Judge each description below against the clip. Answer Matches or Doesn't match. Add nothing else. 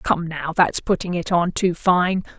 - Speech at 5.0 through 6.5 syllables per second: Doesn't match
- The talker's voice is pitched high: Doesn't match